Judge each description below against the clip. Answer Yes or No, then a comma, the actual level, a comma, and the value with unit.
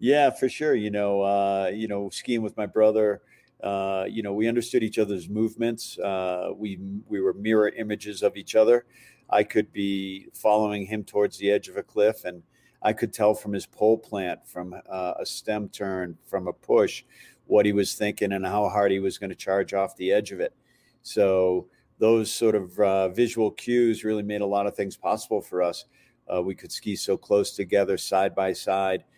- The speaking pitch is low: Yes, low, 105 Hz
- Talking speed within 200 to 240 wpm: Yes, fast, 205 wpm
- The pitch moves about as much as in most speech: No, narrow, 2.1 semitones